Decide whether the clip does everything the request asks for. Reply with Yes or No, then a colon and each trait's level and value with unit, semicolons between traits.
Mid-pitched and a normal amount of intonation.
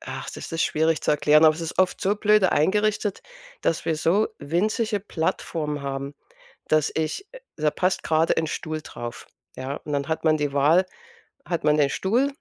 Yes: medium, 160 Hz; average, 4.0 semitones